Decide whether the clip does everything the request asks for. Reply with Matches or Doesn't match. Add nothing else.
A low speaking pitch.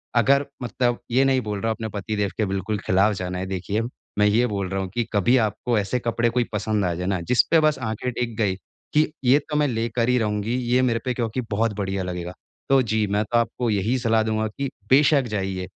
Matches